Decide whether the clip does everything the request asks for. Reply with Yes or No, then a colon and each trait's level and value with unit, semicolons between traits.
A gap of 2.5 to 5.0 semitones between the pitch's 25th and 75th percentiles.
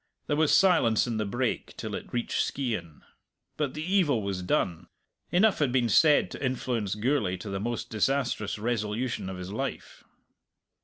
No: wide, 5.4 semitones